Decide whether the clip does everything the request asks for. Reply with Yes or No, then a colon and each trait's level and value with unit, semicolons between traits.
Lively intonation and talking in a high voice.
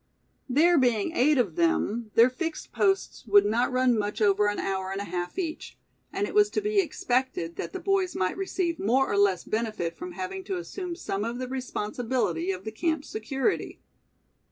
Yes: wide, 8.7 semitones; high, 245 Hz